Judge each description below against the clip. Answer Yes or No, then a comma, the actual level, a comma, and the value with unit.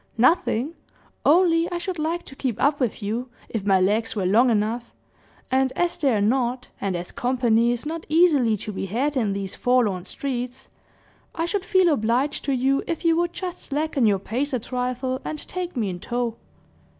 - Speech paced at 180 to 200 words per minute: Yes, average, 185 wpm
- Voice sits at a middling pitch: No, very high, 255 Hz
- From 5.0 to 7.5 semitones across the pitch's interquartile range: Yes, wide, 5.6 semitones